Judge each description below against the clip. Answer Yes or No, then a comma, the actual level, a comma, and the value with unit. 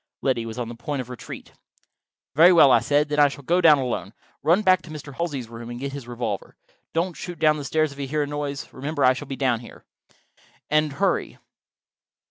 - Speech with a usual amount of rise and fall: Yes, average, 3.4 semitones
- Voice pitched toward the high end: No, medium, 140 Hz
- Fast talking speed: Yes, fast, 215 wpm